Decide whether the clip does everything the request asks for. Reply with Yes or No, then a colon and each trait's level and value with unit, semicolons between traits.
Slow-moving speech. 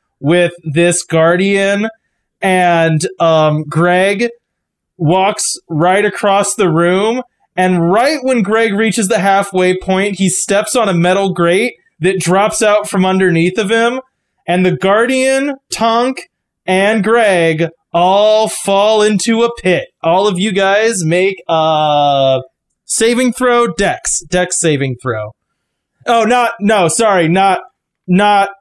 Yes: slow, 130 wpm